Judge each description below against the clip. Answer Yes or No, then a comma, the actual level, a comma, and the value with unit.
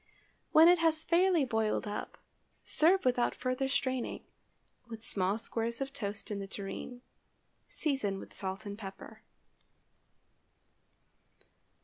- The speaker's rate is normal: No, slow, 115 wpm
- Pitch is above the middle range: Yes, high, 240 Hz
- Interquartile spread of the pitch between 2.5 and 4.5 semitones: No, average, 5.3 semitones